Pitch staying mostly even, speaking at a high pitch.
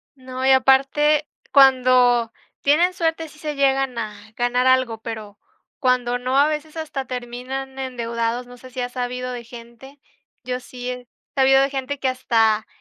Yes: narrow, 1.8 semitones; very high, 255 Hz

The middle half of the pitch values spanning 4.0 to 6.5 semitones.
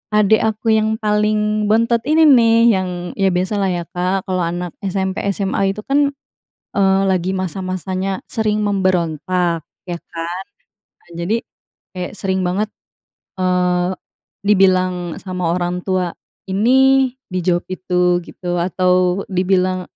No: average, 2.7 semitones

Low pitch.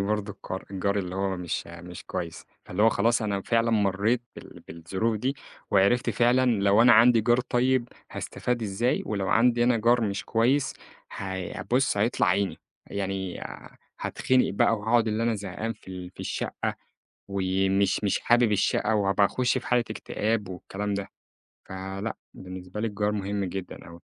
Yes: low, 105 Hz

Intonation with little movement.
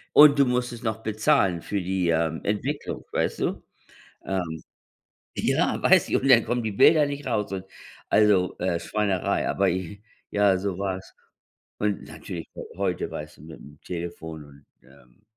No: average, 4.3 semitones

